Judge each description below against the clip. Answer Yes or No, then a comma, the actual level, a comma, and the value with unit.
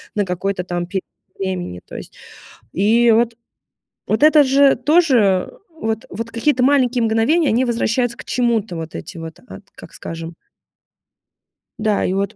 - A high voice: Yes, high, 225 Hz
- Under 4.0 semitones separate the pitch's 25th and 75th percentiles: No, average, 5.0 semitones